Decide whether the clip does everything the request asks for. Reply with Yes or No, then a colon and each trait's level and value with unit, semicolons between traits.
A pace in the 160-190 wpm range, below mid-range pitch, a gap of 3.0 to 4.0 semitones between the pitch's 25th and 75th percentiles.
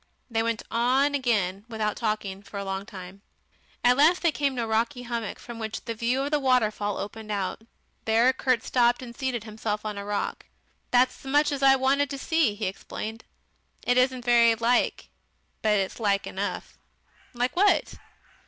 No: average, 180 wpm; high, 235 Hz; average, 3.5 semitones